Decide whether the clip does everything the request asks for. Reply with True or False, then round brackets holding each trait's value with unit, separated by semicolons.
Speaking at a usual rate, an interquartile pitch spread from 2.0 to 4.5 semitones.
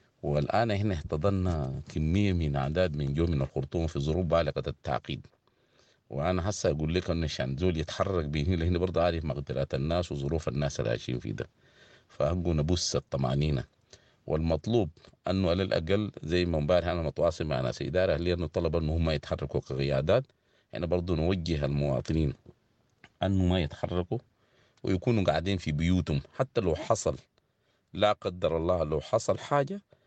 True (150 wpm; 3.7 semitones)